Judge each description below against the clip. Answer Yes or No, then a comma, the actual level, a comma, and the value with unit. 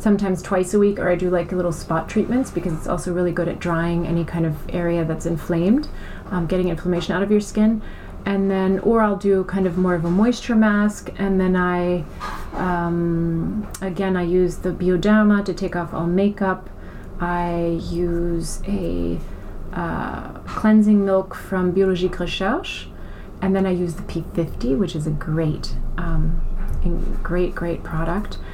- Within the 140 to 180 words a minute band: Yes, average, 170 wpm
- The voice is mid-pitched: Yes, medium, 180 Hz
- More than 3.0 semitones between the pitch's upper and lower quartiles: No, narrow, 2.5 semitones